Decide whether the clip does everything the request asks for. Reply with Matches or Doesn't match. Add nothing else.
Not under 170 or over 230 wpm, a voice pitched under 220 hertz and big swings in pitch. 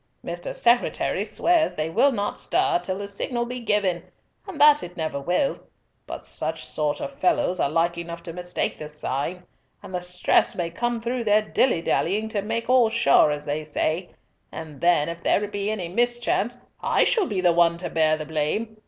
Matches